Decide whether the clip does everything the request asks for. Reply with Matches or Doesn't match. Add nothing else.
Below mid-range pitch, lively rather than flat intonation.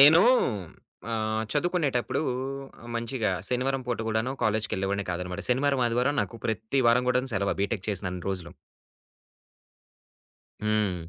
Doesn't match